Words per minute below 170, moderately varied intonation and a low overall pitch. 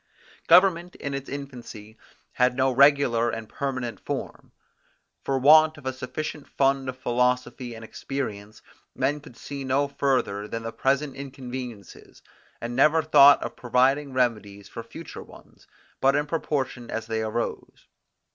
Yes: average, 145 wpm; average, 3.0 semitones; low, 130 Hz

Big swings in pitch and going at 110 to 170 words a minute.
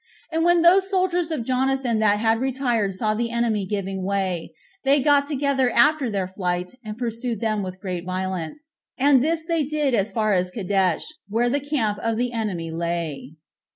No: wide, 6.4 semitones; average, 180 wpm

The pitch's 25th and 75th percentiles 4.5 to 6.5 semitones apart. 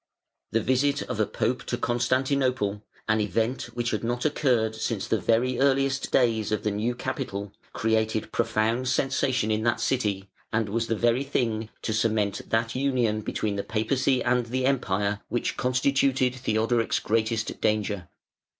No: average, 2.9 semitones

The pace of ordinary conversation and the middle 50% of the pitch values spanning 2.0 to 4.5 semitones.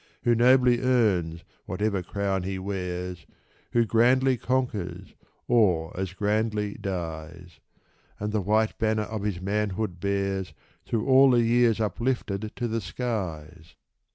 No: slow, 125 wpm; average, 4.1 semitones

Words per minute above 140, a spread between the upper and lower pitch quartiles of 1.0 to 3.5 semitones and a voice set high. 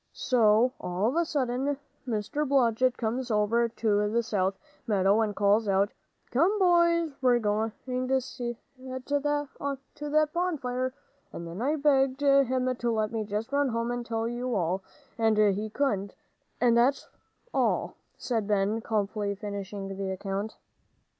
No: average, 150 wpm; average, 4.4 semitones; high, 235 Hz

